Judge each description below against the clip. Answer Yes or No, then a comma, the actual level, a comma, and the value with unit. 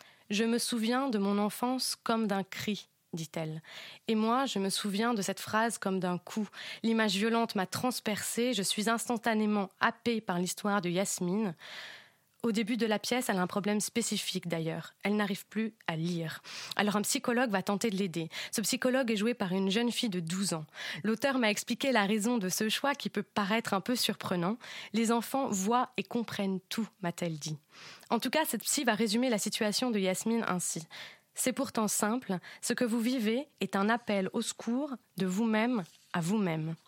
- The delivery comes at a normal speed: Yes, average, 190 wpm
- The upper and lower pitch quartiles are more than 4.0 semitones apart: No, average, 3.4 semitones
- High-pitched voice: Yes, high, 215 Hz